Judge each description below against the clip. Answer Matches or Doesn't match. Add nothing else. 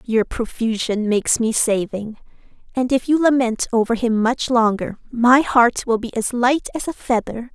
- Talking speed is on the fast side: Doesn't match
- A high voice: Matches